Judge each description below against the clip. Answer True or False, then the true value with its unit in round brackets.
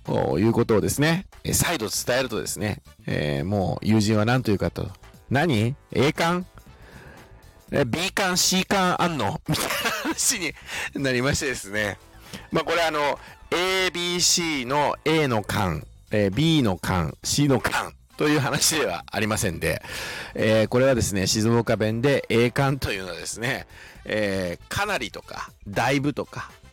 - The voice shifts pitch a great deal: True (6.3 semitones)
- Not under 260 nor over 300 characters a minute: True (270 characters per minute)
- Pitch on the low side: True (120 Hz)